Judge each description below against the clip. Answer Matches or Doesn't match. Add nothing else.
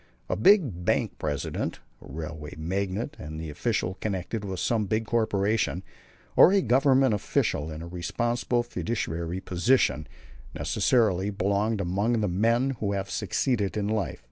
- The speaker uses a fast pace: Doesn't match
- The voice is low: Matches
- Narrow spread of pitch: Doesn't match